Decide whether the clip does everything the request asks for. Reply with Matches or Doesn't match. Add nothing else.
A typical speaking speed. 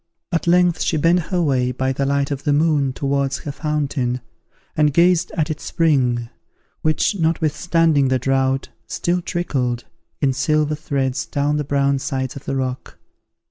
Matches